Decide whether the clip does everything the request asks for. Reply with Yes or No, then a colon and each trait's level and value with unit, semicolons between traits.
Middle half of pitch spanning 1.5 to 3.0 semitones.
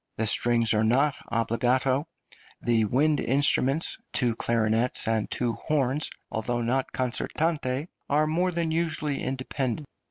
No: average, 4.1 semitones